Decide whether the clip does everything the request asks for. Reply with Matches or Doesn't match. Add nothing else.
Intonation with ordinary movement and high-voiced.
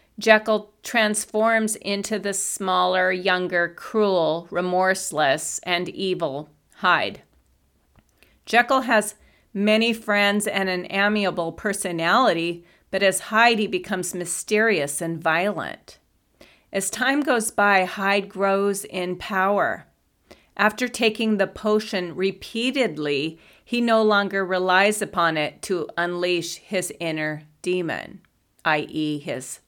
Matches